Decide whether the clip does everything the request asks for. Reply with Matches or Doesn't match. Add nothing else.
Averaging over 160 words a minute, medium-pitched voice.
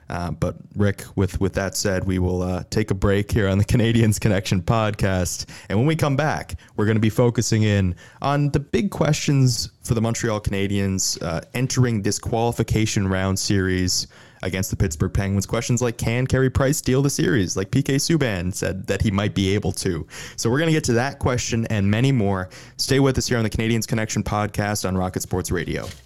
Doesn't match